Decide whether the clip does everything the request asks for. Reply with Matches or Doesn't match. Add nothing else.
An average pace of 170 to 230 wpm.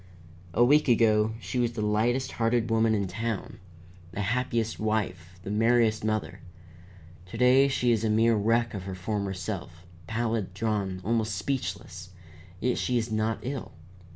Doesn't match